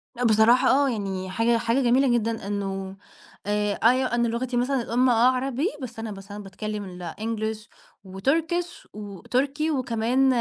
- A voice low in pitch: No, high, 230 Hz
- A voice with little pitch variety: No, average, 3.7 semitones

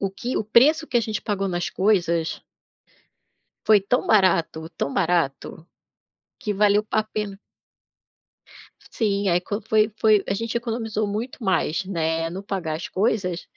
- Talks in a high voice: Yes, high, 200 Hz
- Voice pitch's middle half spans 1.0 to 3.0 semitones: No, average, 3.6 semitones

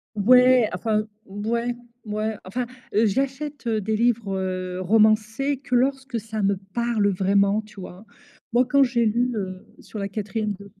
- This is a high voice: Yes, high, 220 Hz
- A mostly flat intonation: No, average, 3.3 semitones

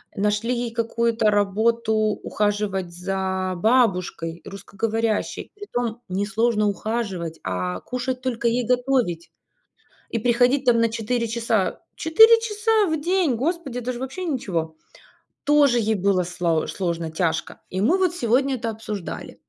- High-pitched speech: Yes, high, 225 Hz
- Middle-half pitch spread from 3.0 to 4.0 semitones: No, average, 4.5 semitones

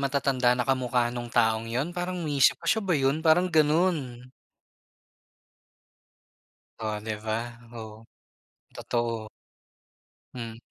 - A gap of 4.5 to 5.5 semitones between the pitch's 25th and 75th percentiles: Yes, average, 5.0 semitones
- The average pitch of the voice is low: Yes, low, 130 Hz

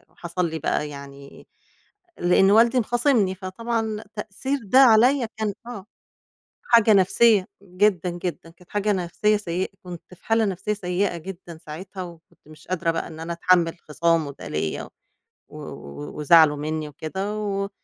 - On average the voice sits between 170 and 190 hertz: Yes, medium, 185 Hz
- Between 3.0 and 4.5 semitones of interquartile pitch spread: Yes, average, 4.1 semitones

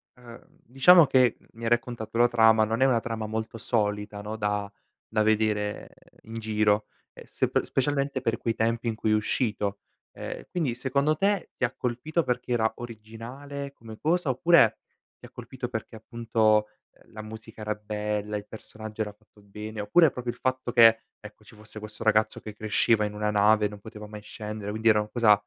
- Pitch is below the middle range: Yes, low, 110 Hz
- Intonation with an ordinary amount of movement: No, narrow, 2.3 semitones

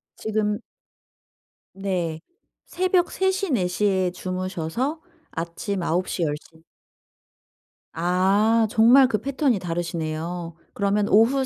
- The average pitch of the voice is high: Yes, high, 195 Hz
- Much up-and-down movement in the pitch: No, average, 4.8 semitones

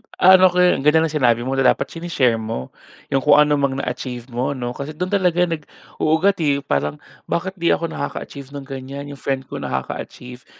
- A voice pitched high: No, medium, 140 Hz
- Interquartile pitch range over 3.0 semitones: Yes, average, 4.6 semitones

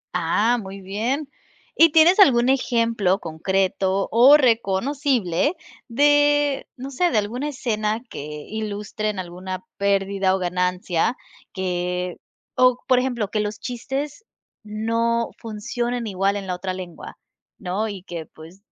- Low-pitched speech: No, high, 215 Hz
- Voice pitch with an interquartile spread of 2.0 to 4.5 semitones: No, average, 4.9 semitones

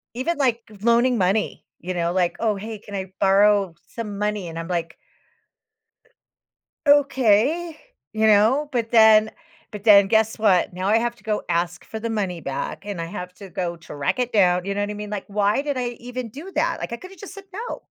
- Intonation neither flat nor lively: Yes, average, 4.0 semitones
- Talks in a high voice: Yes, high, 210 Hz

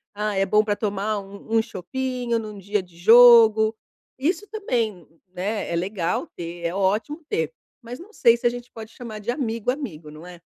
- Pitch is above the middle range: Yes, high, 215 Hz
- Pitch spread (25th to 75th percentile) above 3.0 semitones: Yes, average, 3.9 semitones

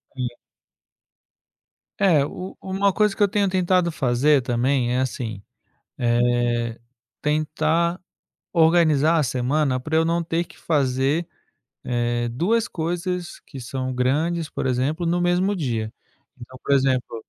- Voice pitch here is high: No, medium, 150 Hz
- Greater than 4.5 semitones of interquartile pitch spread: Yes, wide, 5.4 semitones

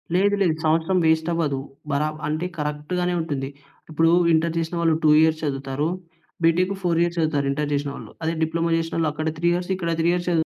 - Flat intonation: Yes, narrow, 2.0 semitones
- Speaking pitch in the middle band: Yes, medium, 160 Hz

